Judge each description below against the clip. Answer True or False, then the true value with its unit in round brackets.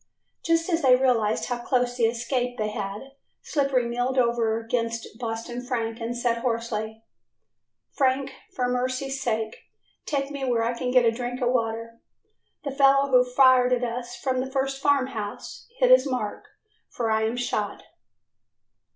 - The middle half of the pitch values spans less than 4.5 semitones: True (2.4 semitones)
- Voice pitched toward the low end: False (245 Hz)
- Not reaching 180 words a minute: True (160 wpm)